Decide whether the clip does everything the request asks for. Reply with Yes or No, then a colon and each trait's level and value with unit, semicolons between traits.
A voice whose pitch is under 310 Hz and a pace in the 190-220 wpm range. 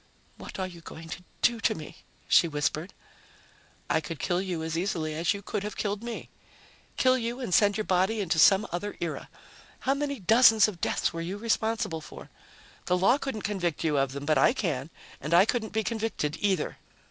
Yes: high, 190 Hz; average, 200 wpm